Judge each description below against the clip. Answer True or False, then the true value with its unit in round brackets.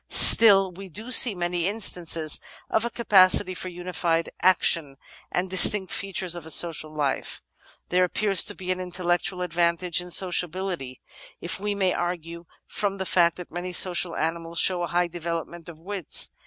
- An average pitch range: False (1.9 semitones)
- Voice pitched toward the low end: False (180 Hz)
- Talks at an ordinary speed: True (170 wpm)